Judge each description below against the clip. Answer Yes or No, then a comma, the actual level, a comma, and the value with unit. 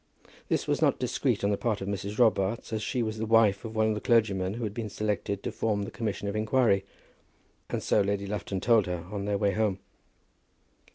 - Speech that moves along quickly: Yes, fast, 220 wpm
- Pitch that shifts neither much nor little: No, narrow, 1.8 semitones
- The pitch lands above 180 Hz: No, low, 105 Hz